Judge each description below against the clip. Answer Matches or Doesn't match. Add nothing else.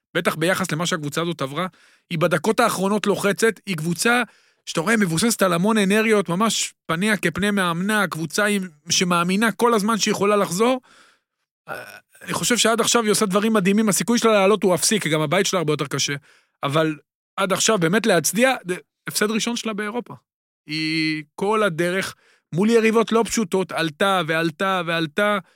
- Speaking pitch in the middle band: Doesn't match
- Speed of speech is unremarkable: Doesn't match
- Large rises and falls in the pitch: Doesn't match